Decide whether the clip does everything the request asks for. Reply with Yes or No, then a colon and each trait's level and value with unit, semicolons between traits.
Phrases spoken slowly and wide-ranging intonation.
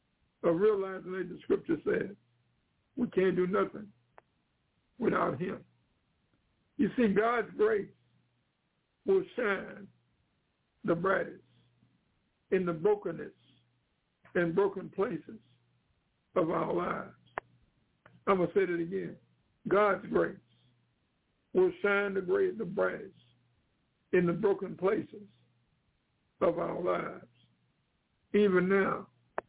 No: slow, 100 wpm; average, 3.4 semitones